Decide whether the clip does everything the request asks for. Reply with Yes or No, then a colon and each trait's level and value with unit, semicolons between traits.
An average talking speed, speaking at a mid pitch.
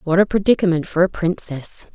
Yes: average, 185 wpm; medium, 175 Hz